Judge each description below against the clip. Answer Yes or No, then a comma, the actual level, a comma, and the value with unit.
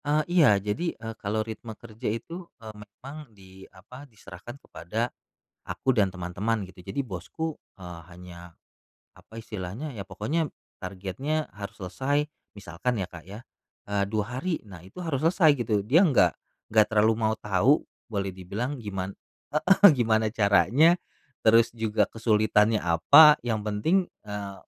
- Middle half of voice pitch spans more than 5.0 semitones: Yes, wide, 5.4 semitones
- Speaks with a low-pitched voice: Yes, low, 110 Hz